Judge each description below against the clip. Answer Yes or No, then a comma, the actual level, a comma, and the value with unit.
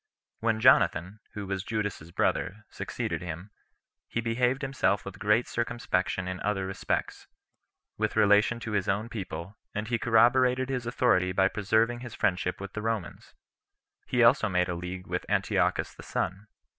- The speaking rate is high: No, average, 155 wpm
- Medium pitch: No, low, 105 Hz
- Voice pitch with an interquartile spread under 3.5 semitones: No, average, 3.8 semitones